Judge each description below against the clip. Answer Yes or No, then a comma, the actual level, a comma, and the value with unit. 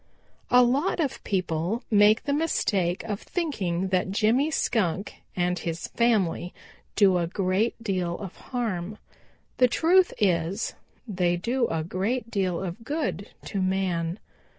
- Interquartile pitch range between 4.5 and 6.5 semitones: Yes, average, 5.0 semitones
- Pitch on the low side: No, high, 195 Hz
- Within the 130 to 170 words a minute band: Yes, slow, 135 wpm